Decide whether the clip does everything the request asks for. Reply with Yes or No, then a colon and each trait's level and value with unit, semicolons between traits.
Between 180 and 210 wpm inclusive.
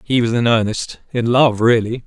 Yes: fast, 205 wpm